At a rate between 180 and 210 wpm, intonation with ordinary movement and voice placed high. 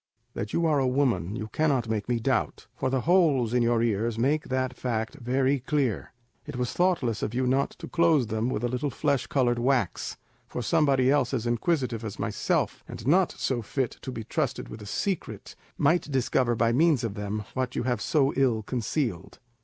No: average, 200 wpm; average, 3.3 semitones; low, 125 Hz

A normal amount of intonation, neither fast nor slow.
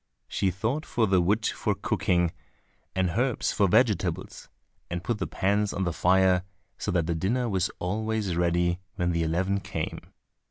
Yes: average, 3.2 semitones; average, 165 wpm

